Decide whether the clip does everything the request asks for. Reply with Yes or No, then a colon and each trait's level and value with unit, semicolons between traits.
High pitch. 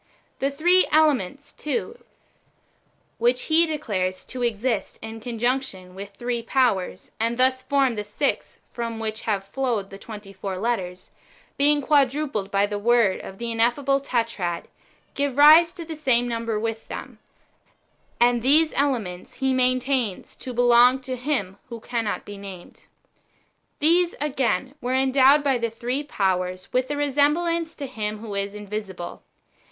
Yes: high, 240 Hz